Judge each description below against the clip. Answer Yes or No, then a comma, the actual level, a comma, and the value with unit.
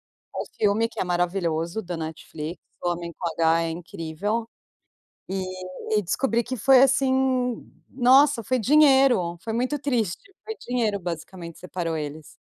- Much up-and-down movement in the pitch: Yes, wide, 6.7 semitones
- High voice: Yes, high, 200 Hz